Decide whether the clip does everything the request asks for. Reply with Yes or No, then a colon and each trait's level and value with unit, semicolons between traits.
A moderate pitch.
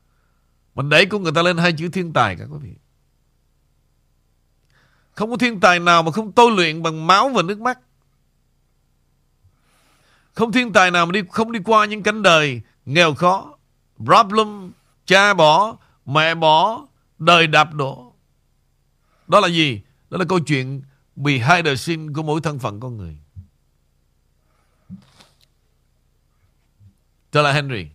Yes: medium, 160 Hz